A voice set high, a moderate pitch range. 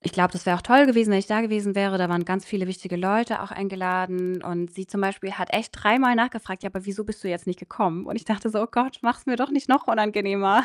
Yes: high, 200 Hz; average, 3.4 semitones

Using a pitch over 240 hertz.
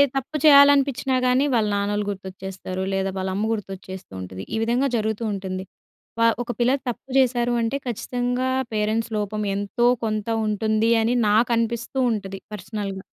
No: high, 220 Hz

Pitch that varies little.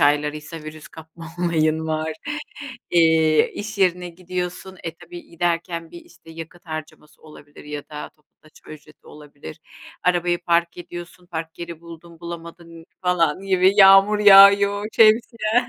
Yes: narrow, 2.2 semitones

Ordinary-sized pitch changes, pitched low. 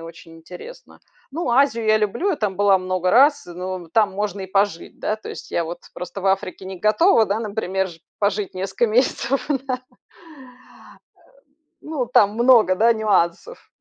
No: average, 4.2 semitones; high, 205 Hz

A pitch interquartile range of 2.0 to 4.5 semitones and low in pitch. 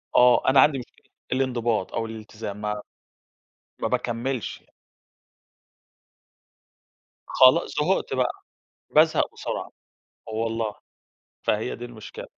Yes: average, 2.7 semitones; low, 120 Hz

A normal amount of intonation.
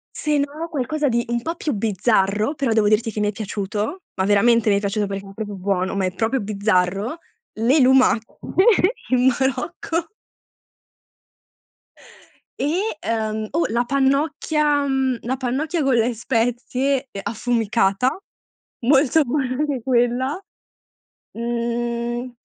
Yes: average, 4.3 semitones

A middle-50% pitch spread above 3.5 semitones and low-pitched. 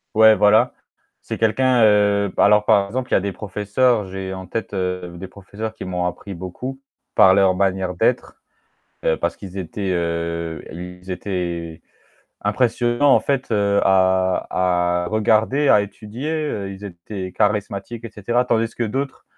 No: average, 3.2 semitones; low, 100 Hz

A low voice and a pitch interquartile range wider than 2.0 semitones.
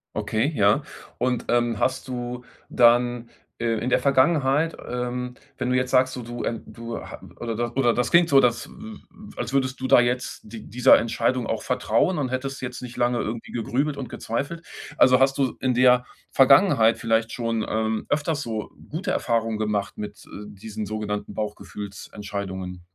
Yes: low, 120 Hz; narrow, 2.5 semitones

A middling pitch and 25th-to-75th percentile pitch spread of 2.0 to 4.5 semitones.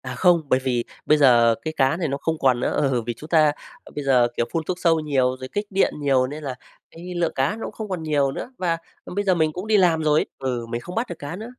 No: medium, 155 Hz; average, 5.0 semitones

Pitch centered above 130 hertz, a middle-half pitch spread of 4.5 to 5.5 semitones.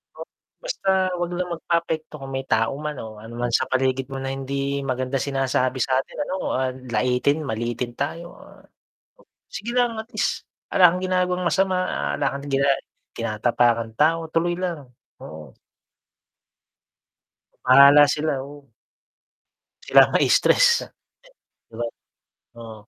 Yes: medium, 140 Hz; average, 5.0 semitones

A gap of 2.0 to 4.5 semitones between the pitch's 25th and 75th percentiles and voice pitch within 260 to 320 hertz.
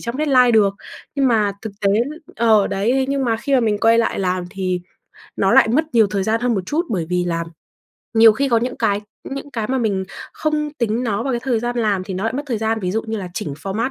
No: average, 3.8 semitones; high, 225 Hz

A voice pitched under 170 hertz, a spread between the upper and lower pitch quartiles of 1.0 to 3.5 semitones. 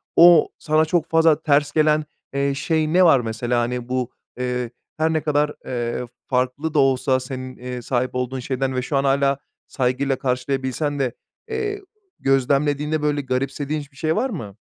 Yes: low, 135 Hz; average, 3.1 semitones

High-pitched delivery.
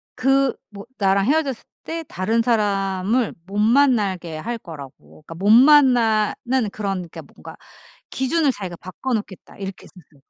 Yes: high, 215 Hz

